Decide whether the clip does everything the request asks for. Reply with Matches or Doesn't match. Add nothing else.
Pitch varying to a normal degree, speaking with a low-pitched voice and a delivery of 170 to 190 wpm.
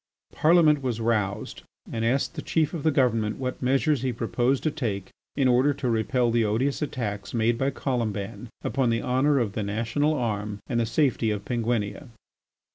Matches